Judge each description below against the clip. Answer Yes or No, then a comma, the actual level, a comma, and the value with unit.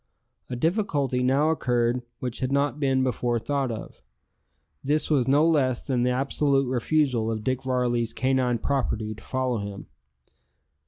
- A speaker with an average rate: Yes, average, 150 wpm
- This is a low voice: Yes, low, 130 Hz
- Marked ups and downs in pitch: No, narrow, 2.5 semitones